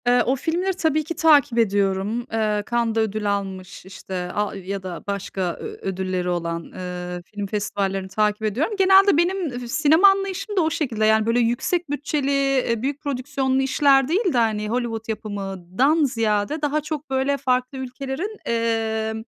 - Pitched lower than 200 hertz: No, high, 240 Hz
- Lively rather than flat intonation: Yes, wide, 6.0 semitones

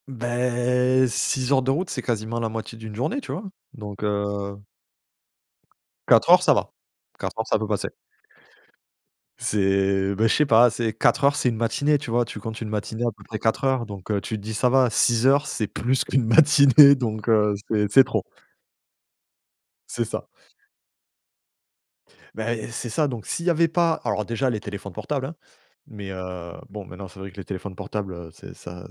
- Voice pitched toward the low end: Yes, low, 110 Hz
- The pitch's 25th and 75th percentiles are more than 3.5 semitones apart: Yes, average, 4.0 semitones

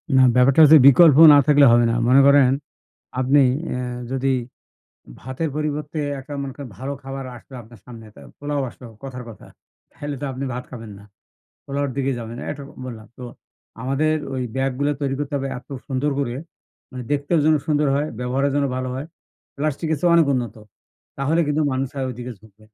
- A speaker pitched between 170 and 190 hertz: No, low, 135 Hz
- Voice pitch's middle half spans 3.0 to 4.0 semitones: No, narrow, 2.4 semitones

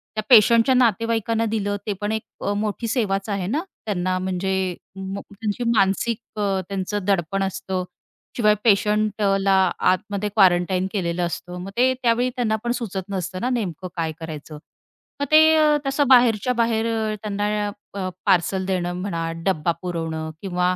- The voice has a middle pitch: No, high, 200 Hz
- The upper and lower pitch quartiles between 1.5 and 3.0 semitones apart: No, average, 3.5 semitones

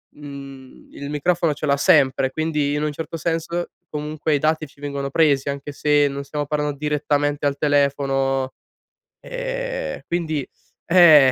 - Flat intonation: Yes, narrow, 2.0 semitones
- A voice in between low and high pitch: Yes, medium, 145 Hz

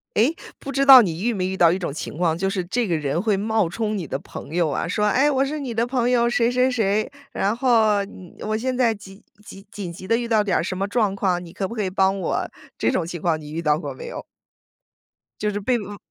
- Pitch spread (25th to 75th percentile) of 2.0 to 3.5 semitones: No, average, 4.5 semitones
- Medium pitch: No, high, 205 Hz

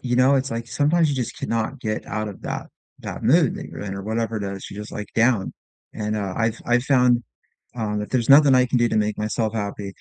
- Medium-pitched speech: No, low, 115 Hz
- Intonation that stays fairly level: No, average, 3.1 semitones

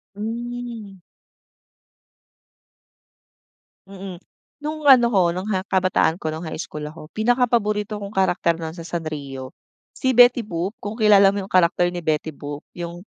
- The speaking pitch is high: Yes, high, 195 Hz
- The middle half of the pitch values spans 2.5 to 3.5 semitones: No, average, 4.7 semitones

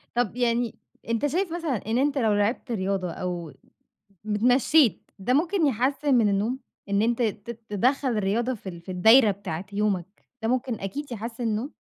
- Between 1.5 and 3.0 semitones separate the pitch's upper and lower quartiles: No, average, 4.3 semitones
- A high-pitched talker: Yes, high, 230 Hz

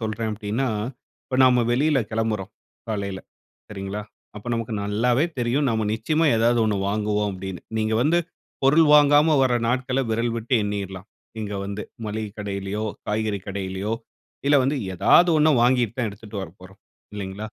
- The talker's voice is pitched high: No, low, 110 Hz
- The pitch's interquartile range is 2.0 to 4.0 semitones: Yes, average, 3.7 semitones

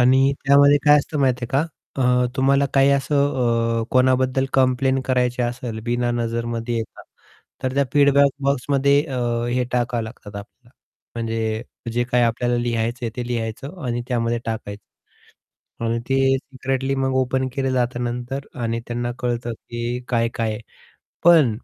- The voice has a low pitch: Yes, low, 125 Hz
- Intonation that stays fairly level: Yes, narrow, 2.2 semitones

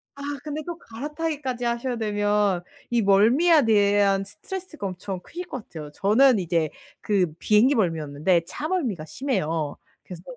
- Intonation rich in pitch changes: Yes, wide, 6.8 semitones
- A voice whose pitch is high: Yes, high, 210 Hz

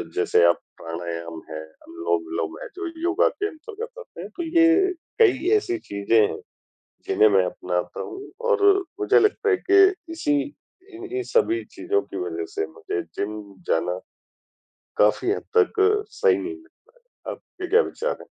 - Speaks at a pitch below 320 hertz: No, very high, 360 Hz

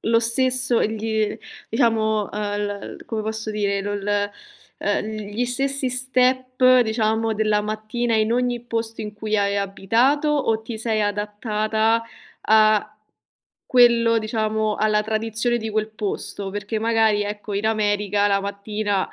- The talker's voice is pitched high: Yes, high, 220 Hz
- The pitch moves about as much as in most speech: No, narrow, 1.8 semitones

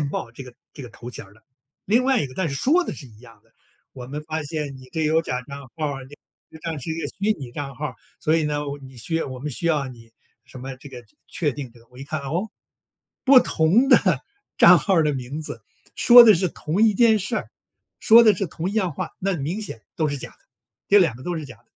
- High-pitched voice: No, medium, 150 Hz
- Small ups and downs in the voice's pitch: No, wide, 5.8 semitones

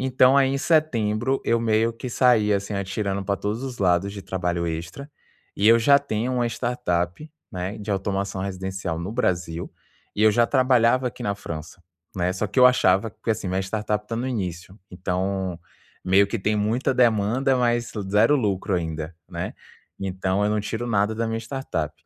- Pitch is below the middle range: Yes, low, 105 Hz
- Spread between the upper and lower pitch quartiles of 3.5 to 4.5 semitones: Yes, average, 4.1 semitones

